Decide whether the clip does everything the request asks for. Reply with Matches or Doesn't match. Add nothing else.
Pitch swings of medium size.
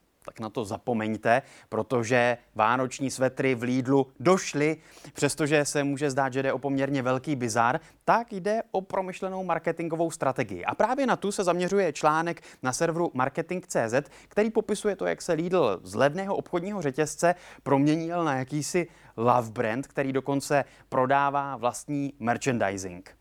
Matches